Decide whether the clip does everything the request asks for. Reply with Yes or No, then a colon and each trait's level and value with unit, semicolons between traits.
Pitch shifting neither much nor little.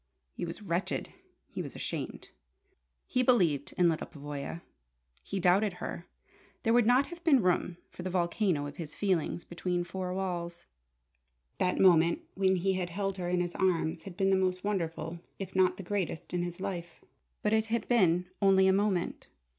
No: narrow, 2.2 semitones